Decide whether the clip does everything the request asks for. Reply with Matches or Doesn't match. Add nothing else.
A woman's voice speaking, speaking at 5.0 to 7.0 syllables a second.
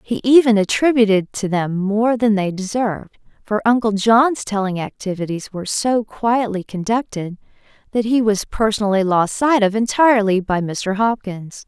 Doesn't match